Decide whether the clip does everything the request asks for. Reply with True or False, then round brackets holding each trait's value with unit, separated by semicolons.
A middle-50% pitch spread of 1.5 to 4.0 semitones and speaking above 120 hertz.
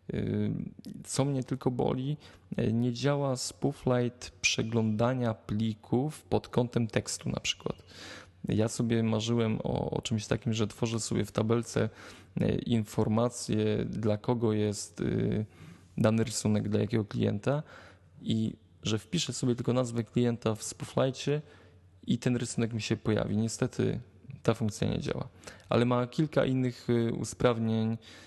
False (2.6 semitones; 115 Hz)